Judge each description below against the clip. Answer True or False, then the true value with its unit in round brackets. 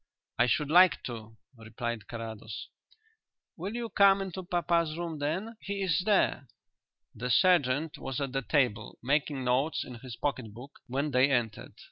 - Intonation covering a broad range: True (6.0 semitones)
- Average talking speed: True (155 wpm)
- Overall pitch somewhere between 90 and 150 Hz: True (140 Hz)